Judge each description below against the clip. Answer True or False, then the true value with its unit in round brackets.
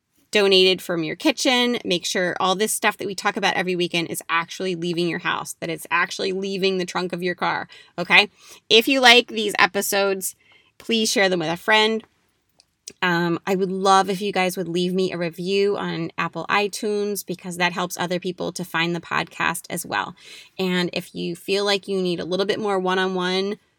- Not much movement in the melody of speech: True (2.1 semitones)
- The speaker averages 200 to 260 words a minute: True (205 wpm)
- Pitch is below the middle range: False (185 Hz)